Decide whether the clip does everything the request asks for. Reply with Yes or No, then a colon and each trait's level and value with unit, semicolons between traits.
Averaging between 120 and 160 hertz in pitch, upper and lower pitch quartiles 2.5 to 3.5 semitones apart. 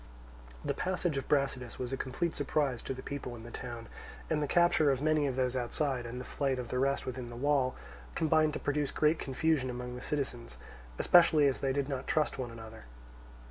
Yes: low, 135 Hz; average, 3.1 semitones